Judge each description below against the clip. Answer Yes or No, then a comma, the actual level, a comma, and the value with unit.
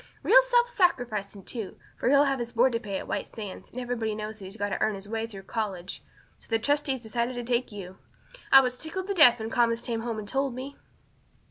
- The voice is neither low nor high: No, high, 235 Hz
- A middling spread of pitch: Yes, average, 3.6 semitones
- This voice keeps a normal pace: No, fast, 235 wpm